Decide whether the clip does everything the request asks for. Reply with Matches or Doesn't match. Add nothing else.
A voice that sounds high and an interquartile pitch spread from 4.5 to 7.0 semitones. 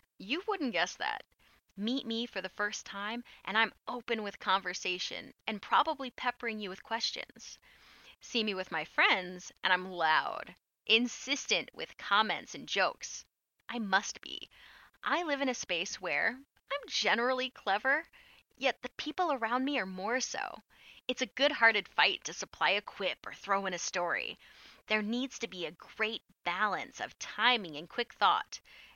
Matches